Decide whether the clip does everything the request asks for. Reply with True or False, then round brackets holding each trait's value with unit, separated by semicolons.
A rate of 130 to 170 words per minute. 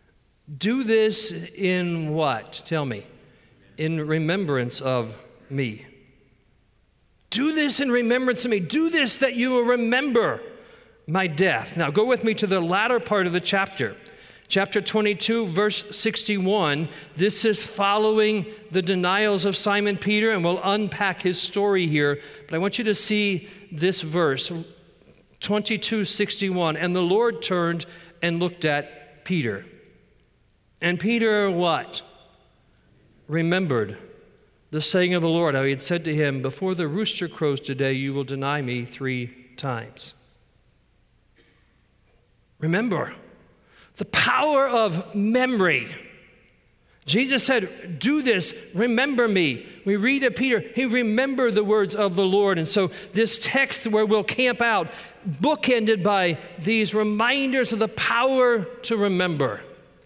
True (135 wpm)